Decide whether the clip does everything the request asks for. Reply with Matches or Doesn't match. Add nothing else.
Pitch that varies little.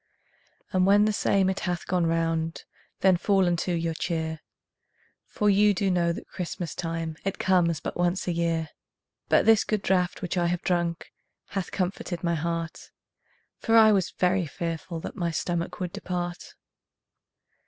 Matches